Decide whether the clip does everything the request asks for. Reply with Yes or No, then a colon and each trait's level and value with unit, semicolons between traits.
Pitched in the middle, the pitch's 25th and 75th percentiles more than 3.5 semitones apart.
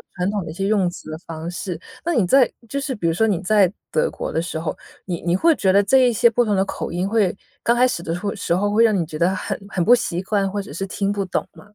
No: high, 195 Hz; average, 4.1 semitones